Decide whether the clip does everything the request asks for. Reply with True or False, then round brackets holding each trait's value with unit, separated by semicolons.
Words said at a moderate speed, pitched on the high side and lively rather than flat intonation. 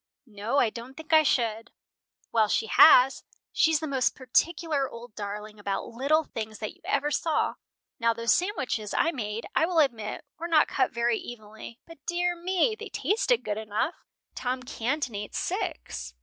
True (170 wpm; 250 Hz; 6.5 semitones)